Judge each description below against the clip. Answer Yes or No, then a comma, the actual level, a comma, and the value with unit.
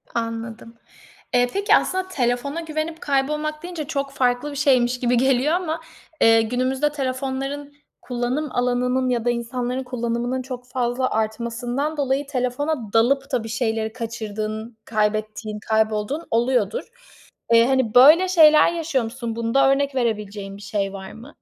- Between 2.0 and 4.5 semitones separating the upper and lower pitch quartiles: Yes, average, 3.5 semitones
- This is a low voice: No, very high, 250 Hz